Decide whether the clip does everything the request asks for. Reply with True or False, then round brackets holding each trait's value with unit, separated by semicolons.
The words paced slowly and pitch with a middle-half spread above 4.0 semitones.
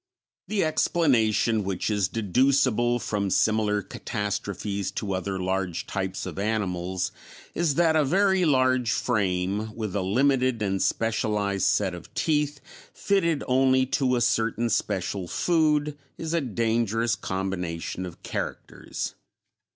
True (125 wpm; 5.5 semitones)